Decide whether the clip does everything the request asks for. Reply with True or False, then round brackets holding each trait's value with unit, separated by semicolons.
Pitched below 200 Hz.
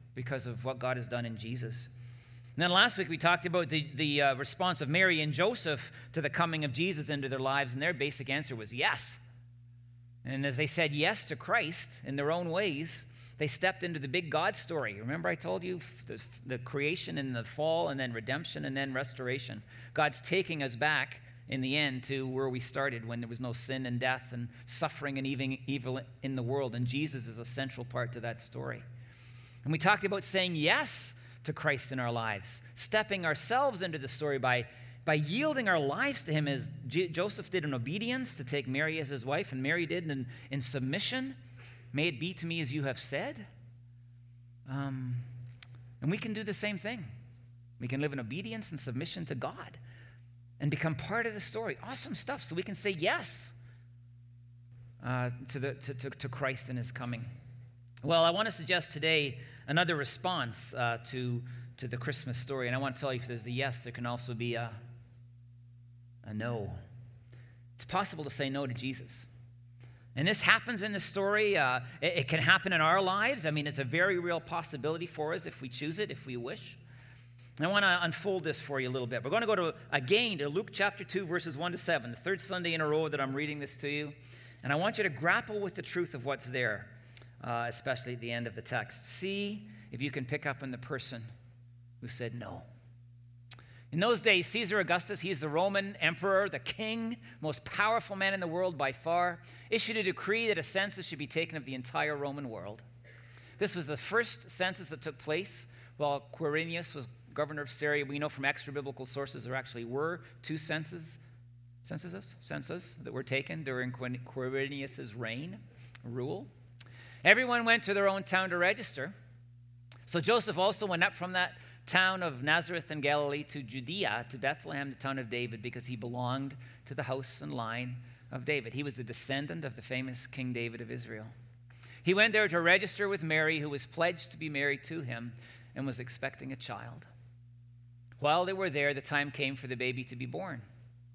True (135 Hz)